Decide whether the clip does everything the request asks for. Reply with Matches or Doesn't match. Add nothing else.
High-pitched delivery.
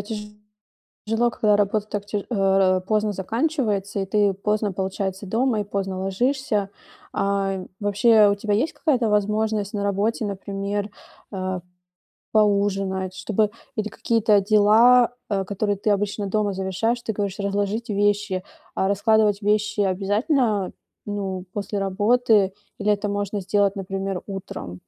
Matches